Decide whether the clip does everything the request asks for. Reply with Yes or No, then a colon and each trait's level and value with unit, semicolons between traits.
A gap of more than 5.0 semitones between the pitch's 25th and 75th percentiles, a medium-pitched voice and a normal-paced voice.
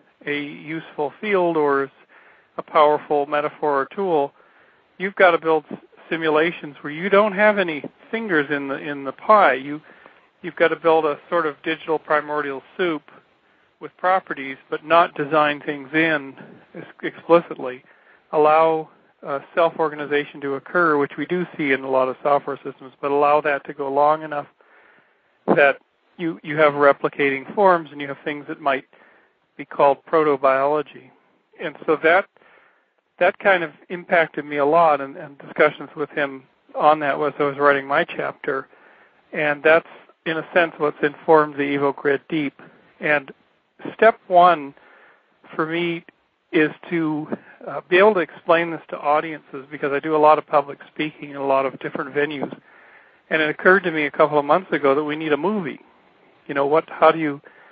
No: average, 2.7 semitones; medium, 155 Hz; average, 170 wpm